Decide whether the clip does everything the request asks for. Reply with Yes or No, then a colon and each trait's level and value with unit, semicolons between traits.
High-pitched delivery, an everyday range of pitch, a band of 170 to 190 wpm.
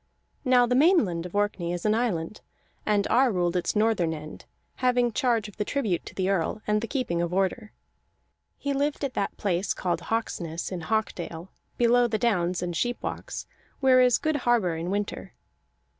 No: high, 210 Hz; wide, 5.7 semitones; average, 175 wpm